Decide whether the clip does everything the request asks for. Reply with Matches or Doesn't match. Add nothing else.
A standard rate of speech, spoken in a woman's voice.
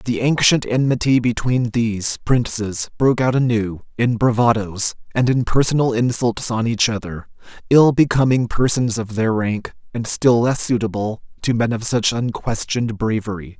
Doesn't match